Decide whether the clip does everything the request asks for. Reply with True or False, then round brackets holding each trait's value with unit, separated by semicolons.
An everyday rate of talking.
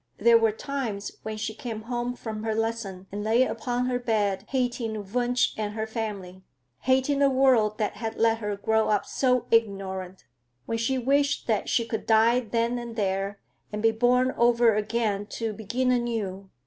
True (175 wpm)